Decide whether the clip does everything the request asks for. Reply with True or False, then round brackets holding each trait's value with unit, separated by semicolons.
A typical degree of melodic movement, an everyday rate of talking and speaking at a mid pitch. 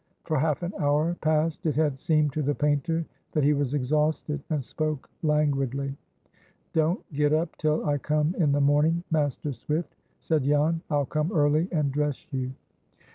False (1.6 semitones; 170 wpm; 150 Hz)